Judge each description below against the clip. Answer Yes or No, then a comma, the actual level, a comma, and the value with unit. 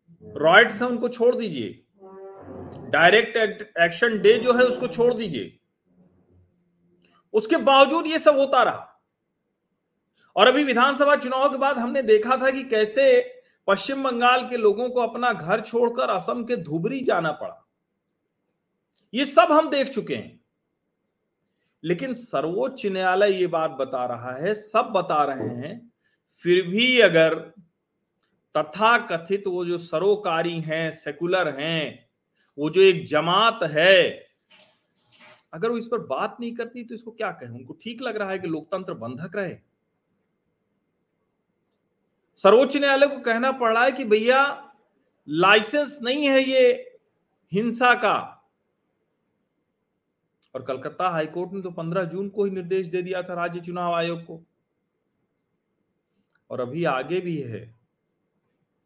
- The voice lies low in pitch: No, high, 210 Hz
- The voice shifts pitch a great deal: Yes, wide, 6.3 semitones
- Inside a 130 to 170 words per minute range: Yes, average, 135 wpm